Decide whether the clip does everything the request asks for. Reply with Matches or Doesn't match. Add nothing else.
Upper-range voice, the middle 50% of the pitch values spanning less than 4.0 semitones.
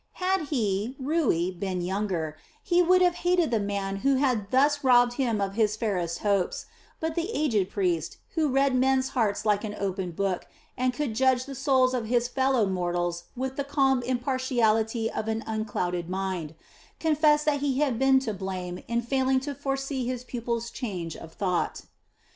Doesn't match